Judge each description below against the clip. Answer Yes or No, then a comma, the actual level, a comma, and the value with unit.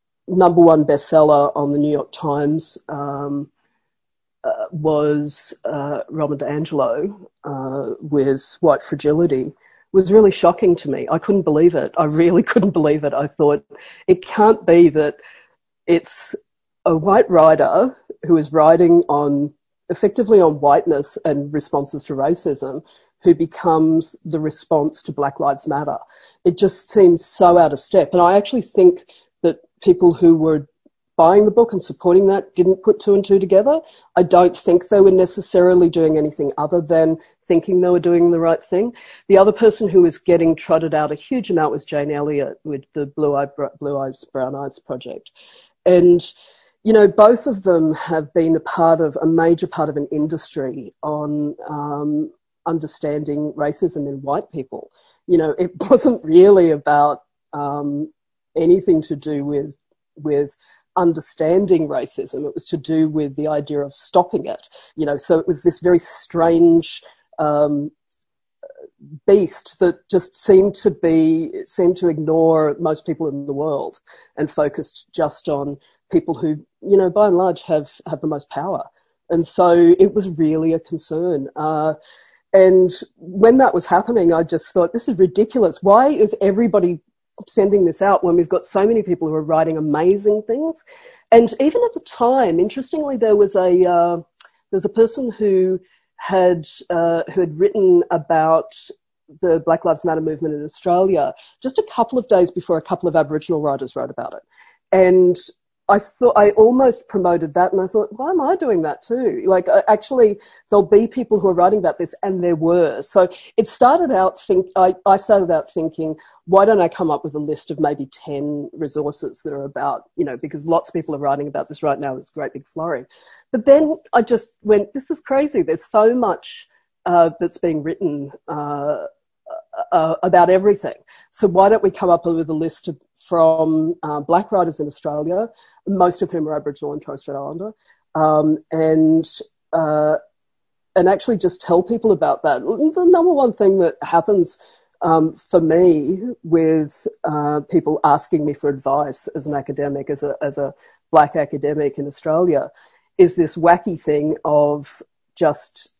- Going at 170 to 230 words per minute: Yes, average, 175 wpm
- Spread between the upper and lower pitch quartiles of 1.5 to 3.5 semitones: No, average, 4.6 semitones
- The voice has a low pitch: No, medium, 170 Hz